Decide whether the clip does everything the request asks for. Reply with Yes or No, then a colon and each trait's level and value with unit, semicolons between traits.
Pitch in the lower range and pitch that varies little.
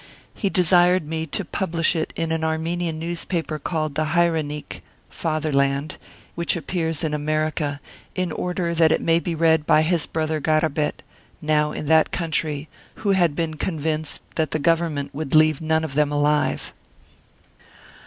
No: medium, 160 Hz; narrow, 1.8 semitones